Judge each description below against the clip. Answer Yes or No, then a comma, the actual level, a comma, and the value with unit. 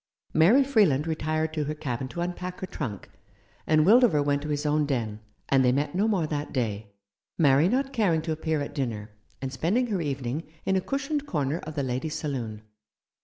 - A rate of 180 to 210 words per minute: Yes, average, 195 wpm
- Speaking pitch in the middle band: Yes, medium, 155 Hz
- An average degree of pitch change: Yes, average, 4.8 semitones